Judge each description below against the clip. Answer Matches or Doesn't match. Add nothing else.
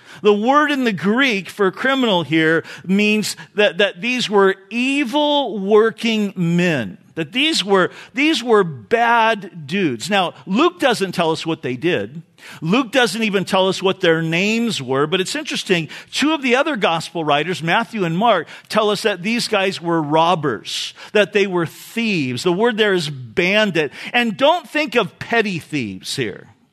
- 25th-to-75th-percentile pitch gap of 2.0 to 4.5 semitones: Doesn't match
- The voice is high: Matches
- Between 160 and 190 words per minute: Matches